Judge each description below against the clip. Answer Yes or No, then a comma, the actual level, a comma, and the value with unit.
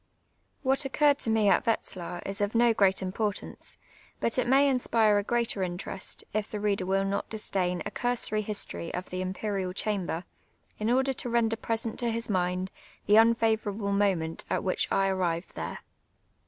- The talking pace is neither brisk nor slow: Yes, average, 180 wpm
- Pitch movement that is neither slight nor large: Yes, average, 3.4 semitones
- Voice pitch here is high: Yes, high, 205 Hz